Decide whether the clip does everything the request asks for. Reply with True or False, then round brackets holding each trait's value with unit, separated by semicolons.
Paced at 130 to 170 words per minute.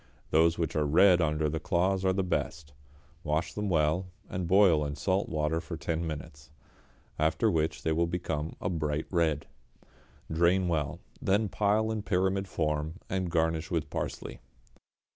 True (160 wpm)